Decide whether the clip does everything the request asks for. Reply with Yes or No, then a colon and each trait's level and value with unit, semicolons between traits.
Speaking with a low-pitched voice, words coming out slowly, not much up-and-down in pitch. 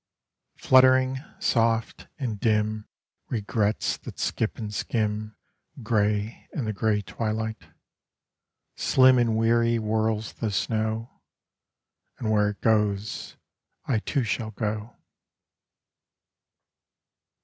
Yes: low, 110 Hz; slow, 95 wpm; narrow, 1.6 semitones